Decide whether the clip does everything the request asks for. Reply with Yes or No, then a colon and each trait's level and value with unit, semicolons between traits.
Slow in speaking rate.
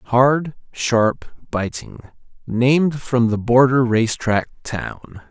Yes: slow, 115 wpm